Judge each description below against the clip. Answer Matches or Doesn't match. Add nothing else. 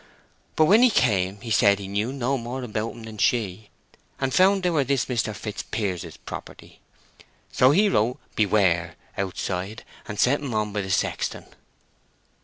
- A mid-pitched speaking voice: Doesn't match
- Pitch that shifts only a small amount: Doesn't match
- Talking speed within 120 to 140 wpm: Doesn't match